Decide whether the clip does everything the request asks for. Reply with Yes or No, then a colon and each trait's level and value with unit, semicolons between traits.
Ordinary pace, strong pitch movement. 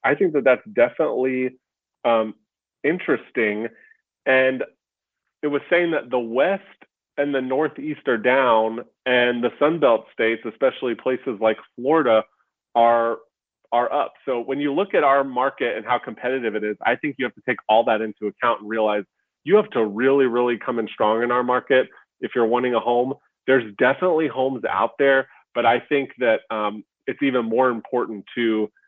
No: average, 175 wpm; average, 3.2 semitones